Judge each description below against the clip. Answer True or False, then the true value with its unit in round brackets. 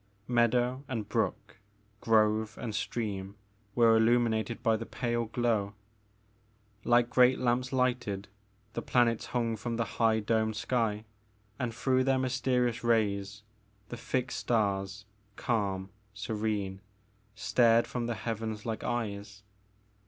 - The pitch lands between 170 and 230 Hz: False (115 Hz)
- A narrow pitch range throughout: True (2.3 semitones)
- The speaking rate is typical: False (120 wpm)